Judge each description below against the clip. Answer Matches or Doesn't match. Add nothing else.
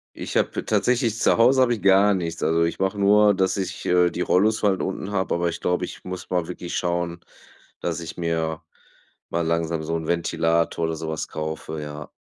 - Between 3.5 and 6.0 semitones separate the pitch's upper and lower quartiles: Doesn't match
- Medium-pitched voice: Doesn't match